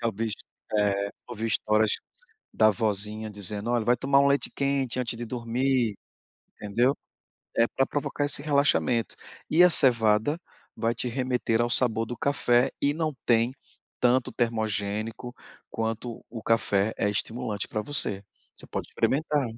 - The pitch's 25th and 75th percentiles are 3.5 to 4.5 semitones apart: No, average, 3.1 semitones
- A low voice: Yes, low, 115 Hz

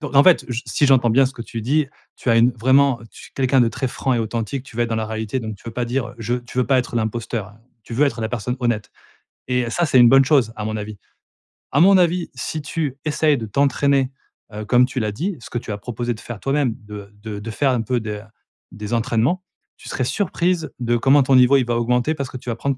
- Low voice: Yes, low, 125 Hz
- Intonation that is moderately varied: Yes, average, 3.3 semitones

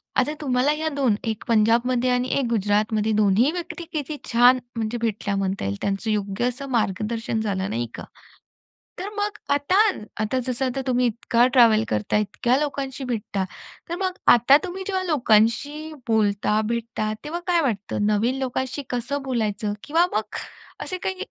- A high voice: Yes, high, 240 Hz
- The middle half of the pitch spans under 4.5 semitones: No, average, 5.0 semitones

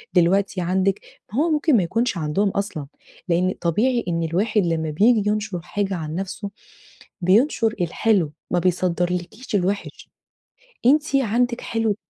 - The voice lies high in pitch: Yes, high, 195 Hz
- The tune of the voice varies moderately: Yes, average, 4.4 semitones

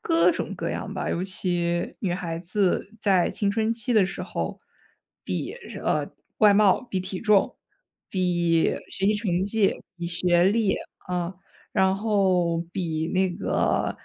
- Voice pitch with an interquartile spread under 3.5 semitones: Yes, average, 2.9 semitones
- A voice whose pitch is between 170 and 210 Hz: Yes, high, 190 Hz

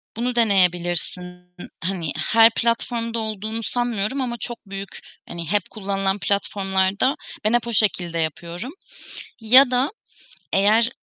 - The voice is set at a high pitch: Yes, high, 205 Hz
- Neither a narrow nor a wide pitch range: Yes, average, 3.9 semitones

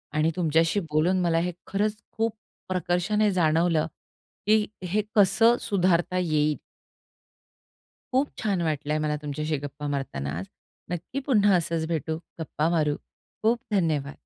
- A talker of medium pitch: Yes, medium, 170 Hz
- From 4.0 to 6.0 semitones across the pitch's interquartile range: Yes, average, 4.6 semitones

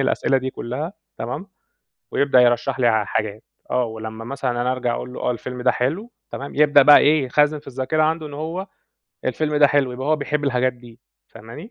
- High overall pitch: No, low, 130 Hz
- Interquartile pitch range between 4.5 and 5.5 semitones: No, average, 3.4 semitones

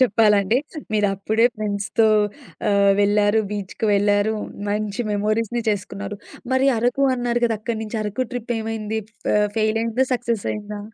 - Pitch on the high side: Yes, high, 215 Hz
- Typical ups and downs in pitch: No, narrow, 1.9 semitones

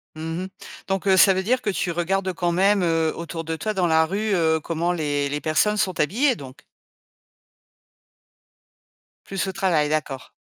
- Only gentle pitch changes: No, average, 3.2 semitones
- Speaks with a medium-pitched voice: Yes, medium, 175 Hz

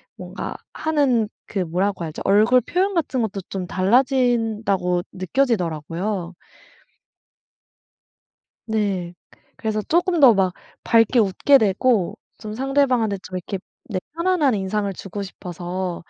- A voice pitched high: Yes, high, 210 Hz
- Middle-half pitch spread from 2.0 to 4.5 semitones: No, average, 5.3 semitones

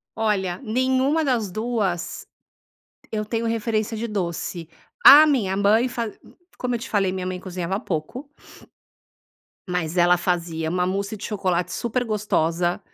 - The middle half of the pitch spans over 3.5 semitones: Yes, average, 4.4 semitones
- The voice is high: Yes, high, 200 Hz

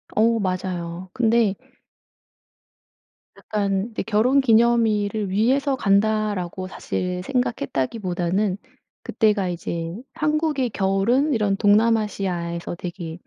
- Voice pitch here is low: No, high, 205 Hz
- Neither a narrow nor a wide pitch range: Yes, average, 3.9 semitones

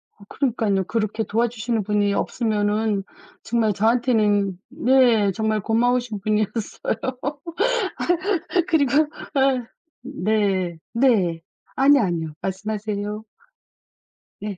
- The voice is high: Yes, high, 215 Hz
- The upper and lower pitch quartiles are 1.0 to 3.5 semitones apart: Yes, average, 3.0 semitones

